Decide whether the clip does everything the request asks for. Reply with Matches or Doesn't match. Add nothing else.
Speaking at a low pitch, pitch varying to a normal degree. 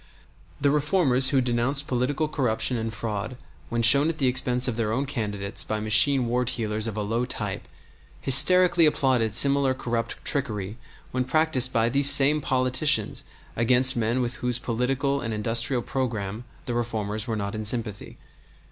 Matches